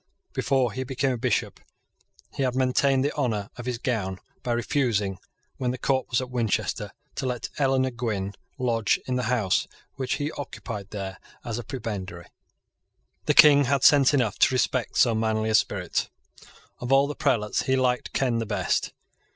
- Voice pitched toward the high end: No, low, 125 Hz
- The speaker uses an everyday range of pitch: Yes, average, 3.1 semitones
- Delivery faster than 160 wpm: Yes, average, 175 wpm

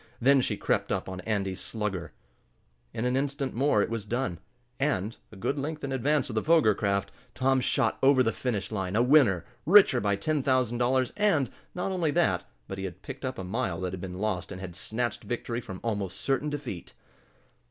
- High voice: No, low, 120 Hz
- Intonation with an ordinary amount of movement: No, wide, 5.7 semitones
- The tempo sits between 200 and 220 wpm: Yes, fast, 205 wpm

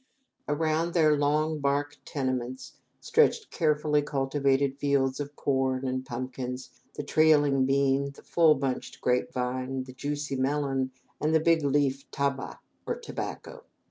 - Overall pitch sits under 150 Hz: Yes, medium, 140 Hz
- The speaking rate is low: Yes, slow, 130 wpm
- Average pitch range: No, narrow, 2.1 semitones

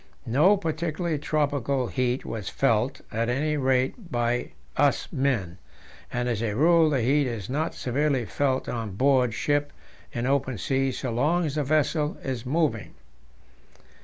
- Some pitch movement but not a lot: Yes, average, 3.6 semitones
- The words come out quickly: No, average, 150 wpm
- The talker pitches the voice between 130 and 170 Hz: Yes, low, 135 Hz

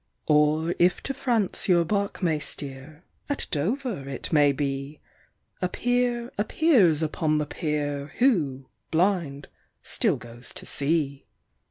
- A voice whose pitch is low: No, medium, 155 Hz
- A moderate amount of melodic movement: No, wide, 5.9 semitones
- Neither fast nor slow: No, slow, 130 wpm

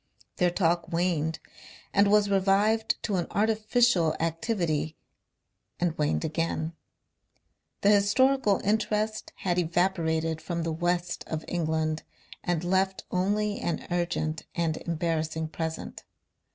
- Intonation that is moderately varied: Yes, average, 3.8 semitones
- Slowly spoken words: Yes, slow, 110 wpm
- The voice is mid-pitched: Yes, medium, 175 Hz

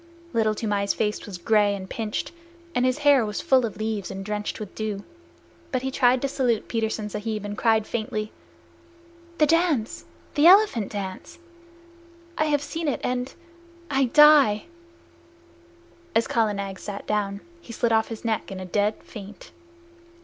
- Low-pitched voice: No, high, 220 Hz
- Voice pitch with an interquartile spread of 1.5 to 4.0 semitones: Yes, average, 3.7 semitones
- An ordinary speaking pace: Yes, average, 160 wpm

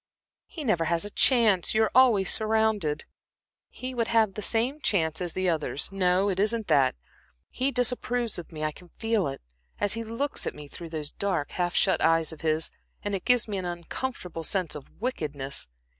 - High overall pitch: Yes, high, 195 Hz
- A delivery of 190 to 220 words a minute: Yes, average, 195 wpm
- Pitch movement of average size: No, wide, 5.7 semitones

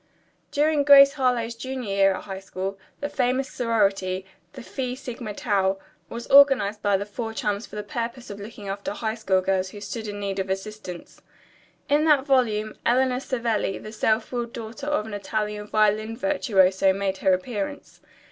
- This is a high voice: Yes, high, 215 Hz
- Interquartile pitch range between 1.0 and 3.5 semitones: No, average, 4.0 semitones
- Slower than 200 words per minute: Yes, average, 175 wpm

